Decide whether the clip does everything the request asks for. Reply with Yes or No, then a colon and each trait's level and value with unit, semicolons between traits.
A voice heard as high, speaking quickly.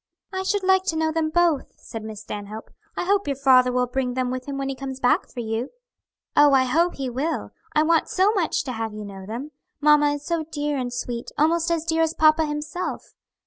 Yes: very high, 290 Hz; fast, 225 wpm